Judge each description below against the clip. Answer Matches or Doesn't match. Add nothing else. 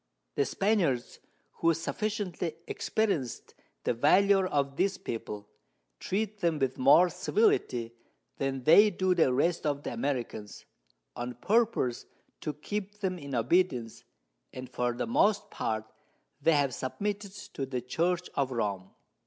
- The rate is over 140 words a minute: Doesn't match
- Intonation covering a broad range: Matches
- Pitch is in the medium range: Matches